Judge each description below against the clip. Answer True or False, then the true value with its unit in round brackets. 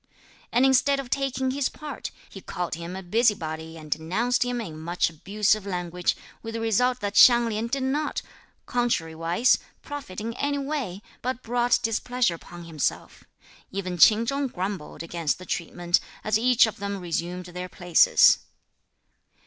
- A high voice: True (210 Hz)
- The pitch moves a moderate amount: False (6.0 semitones)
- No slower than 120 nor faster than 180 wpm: True (155 wpm)